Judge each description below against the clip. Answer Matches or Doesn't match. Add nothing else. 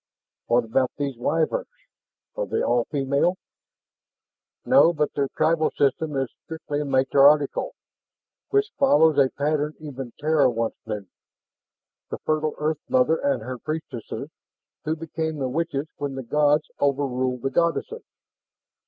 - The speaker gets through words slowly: Matches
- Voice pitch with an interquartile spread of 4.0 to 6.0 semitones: Doesn't match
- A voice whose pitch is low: Doesn't match